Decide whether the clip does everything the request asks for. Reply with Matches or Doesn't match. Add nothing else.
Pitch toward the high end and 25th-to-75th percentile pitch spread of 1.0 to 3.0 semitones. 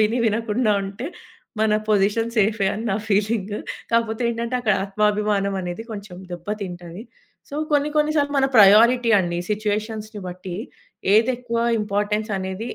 Matches